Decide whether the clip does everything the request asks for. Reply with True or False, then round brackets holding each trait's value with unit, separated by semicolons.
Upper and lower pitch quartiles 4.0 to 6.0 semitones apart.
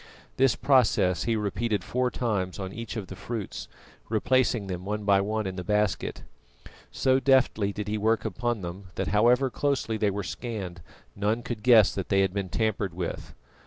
False (3.3 semitones)